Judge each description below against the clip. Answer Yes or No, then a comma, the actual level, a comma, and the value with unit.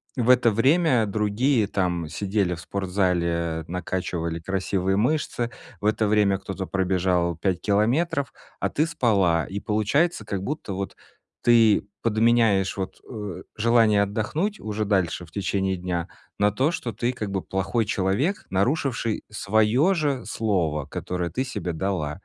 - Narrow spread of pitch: No, average, 4.2 semitones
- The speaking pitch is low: Yes, low, 100 Hz